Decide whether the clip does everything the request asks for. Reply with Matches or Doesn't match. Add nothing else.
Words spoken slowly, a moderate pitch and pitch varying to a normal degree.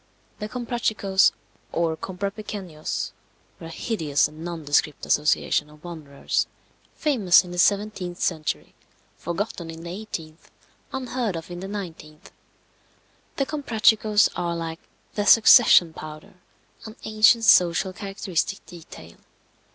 Matches